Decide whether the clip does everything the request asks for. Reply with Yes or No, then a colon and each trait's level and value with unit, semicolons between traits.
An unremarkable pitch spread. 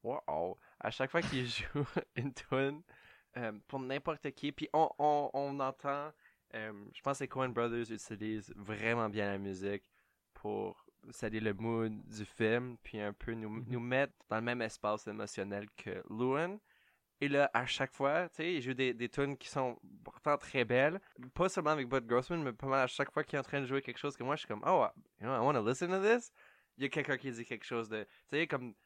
Yes: average, 4.1 semitones